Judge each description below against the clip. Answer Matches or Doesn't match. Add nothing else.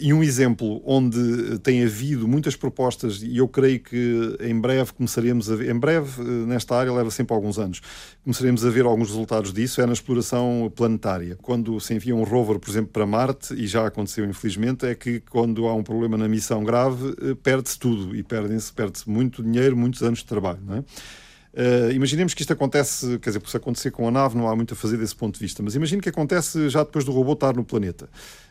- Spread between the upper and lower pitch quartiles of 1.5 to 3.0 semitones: Matches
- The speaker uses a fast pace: Matches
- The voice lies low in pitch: Matches